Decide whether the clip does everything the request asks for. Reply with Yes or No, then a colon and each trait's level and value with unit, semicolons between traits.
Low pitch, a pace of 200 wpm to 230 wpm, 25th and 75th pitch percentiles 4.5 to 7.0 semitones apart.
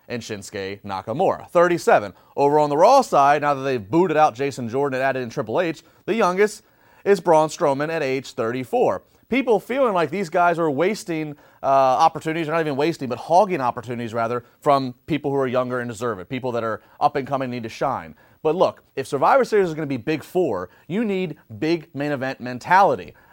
No: medium, 145 Hz; fast, 205 wpm; average, 4.8 semitones